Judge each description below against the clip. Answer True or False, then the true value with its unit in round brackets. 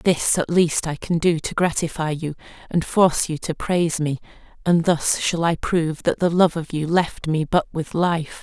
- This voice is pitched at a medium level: True (165 Hz)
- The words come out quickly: True (215 wpm)